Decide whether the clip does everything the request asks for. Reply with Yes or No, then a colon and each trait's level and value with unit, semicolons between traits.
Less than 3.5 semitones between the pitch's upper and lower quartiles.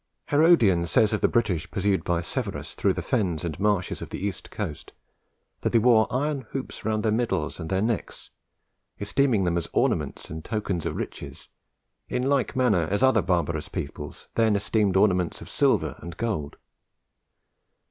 No: average, 5.1 semitones